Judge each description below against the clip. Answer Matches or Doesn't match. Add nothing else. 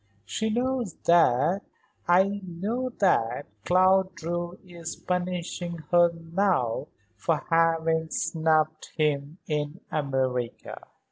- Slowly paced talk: Matches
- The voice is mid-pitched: Matches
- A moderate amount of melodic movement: Matches